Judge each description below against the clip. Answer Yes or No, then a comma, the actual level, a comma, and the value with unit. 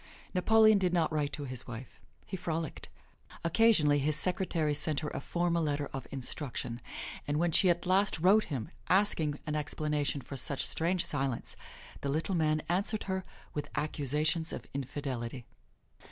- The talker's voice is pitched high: No, medium, 155 Hz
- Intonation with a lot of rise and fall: No, average, 3.6 semitones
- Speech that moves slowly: No, average, 155 wpm